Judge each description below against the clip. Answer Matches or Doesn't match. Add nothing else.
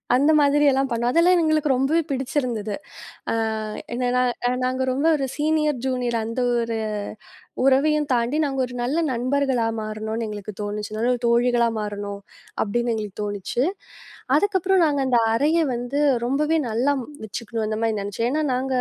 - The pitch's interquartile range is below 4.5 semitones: Matches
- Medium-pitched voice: Doesn't match